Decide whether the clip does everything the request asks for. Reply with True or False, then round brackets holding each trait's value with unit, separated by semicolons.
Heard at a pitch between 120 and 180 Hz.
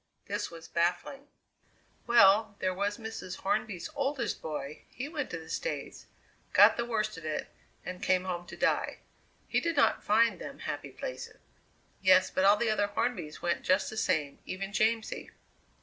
False (200 Hz)